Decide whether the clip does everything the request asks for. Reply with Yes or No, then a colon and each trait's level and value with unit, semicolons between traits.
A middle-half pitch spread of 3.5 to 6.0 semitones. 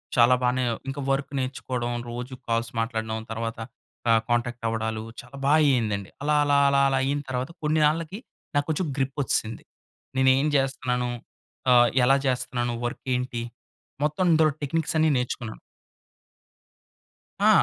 No: average, 3.0 semitones